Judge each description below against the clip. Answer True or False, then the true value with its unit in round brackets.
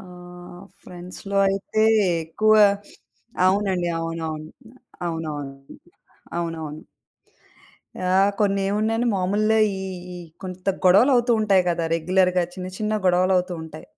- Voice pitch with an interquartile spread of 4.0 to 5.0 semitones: False (3.3 semitones)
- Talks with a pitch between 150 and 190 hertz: True (185 Hz)